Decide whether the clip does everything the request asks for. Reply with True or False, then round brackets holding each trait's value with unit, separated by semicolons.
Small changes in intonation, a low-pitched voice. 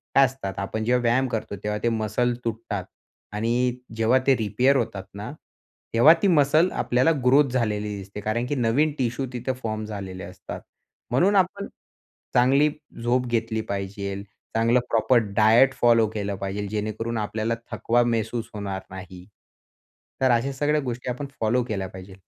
False (3.3 semitones; 115 Hz)